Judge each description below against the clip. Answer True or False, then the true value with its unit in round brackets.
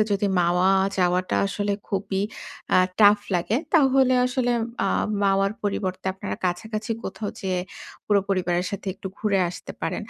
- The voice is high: True (195 Hz)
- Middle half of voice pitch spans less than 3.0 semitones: True (2.4 semitones)